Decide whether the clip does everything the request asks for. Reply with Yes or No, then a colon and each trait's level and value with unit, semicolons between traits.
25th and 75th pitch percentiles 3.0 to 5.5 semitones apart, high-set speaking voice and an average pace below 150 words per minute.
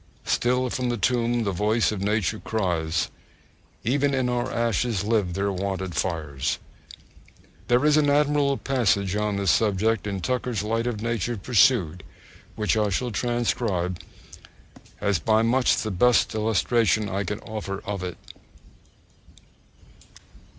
No: average, 3.8 semitones; low, 110 Hz; slow, 135 wpm